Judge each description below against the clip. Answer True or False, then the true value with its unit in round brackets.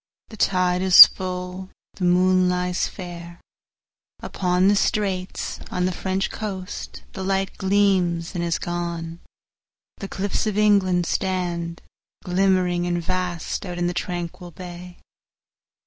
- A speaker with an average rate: False (115 wpm)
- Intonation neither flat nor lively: False (1.4 semitones)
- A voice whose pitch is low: False (180 Hz)